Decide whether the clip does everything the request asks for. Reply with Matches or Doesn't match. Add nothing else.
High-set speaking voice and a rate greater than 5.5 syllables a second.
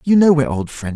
Doesn't match